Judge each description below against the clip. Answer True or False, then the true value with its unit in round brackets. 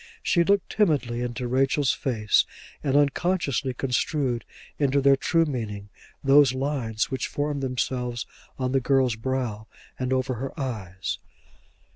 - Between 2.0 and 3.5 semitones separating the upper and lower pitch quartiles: True (2.8 semitones)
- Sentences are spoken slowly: True (130 wpm)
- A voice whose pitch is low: True (130 Hz)